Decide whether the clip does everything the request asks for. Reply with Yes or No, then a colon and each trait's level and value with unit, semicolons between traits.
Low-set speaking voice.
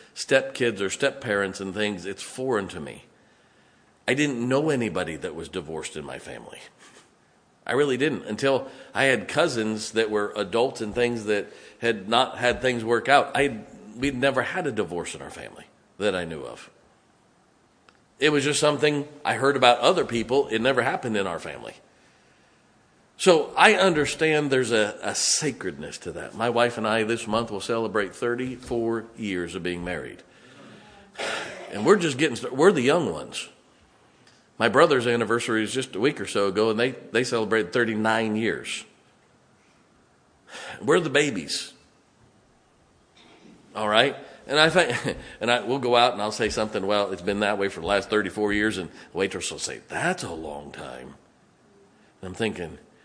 Yes: low, 115 Hz